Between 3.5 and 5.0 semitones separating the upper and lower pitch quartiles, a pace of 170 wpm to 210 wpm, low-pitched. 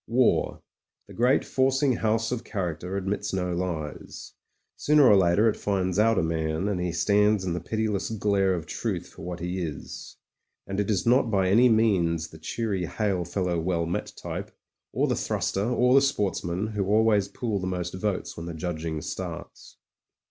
Yes: average, 4.0 semitones; average, 180 wpm; very low, 95 Hz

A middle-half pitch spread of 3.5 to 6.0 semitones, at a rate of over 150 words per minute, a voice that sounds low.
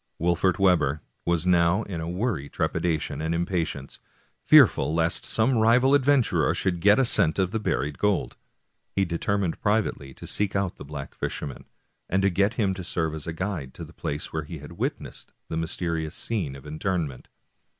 Yes: average, 4.1 semitones; average, 175 wpm; very low, 85 Hz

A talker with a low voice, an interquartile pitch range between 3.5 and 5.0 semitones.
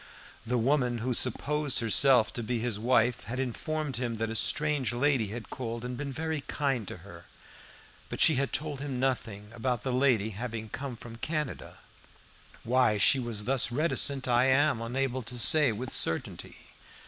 No: low, 125 Hz; average, 3.1 semitones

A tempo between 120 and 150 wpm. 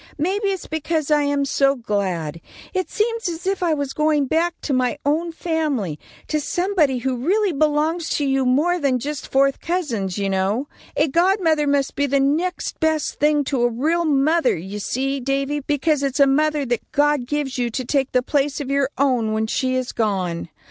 No: average, 195 wpm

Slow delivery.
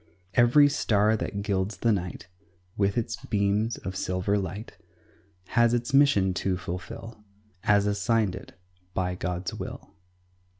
Yes: slow, 130 wpm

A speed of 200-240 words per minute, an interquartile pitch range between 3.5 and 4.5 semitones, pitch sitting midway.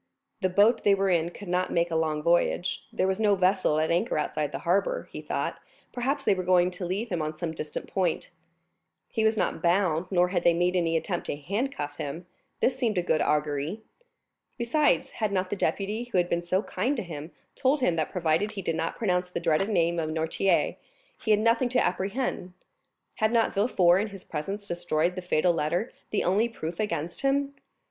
Yes: fast, 205 wpm; average, 4.0 semitones; medium, 180 Hz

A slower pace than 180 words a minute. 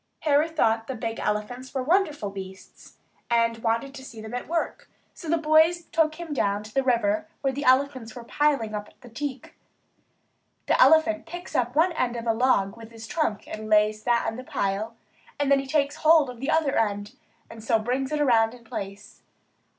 No: average, 195 wpm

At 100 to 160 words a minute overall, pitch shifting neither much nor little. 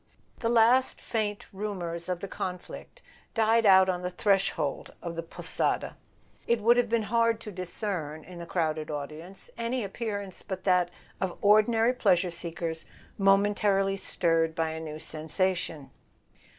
Yes: average, 150 wpm; average, 4.2 semitones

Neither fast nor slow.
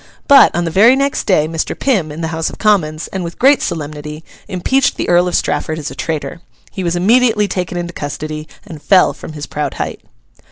No: fast, 210 wpm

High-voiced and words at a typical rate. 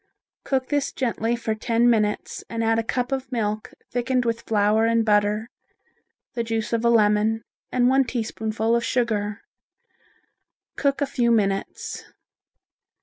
Yes: high, 230 Hz; average, 145 wpm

